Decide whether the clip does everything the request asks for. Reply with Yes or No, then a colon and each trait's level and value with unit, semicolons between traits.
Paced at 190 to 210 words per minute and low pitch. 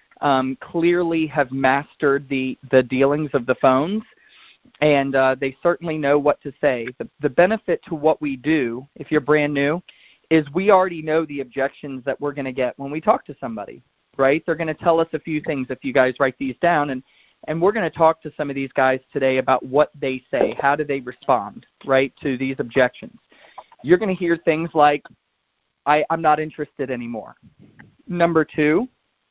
No: average, 200 wpm; medium, 145 Hz